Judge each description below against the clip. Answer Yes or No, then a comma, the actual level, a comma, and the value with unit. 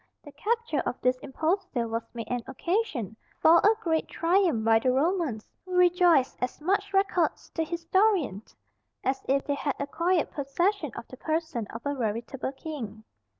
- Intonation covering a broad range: Yes, wide, 6.1 semitones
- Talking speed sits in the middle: Yes, average, 160 wpm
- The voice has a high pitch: Yes, very high, 300 Hz